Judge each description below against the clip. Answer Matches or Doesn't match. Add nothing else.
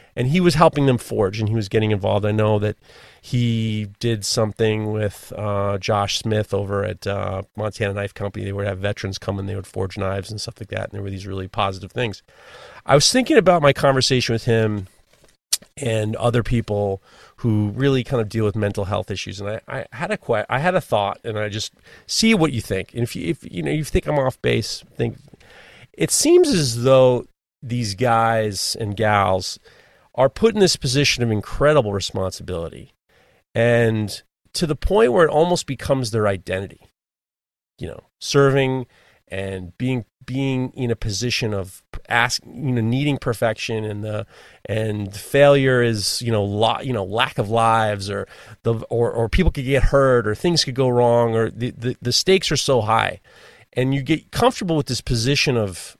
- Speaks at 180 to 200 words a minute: Matches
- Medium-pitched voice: Doesn't match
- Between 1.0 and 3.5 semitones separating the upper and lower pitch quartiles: Doesn't match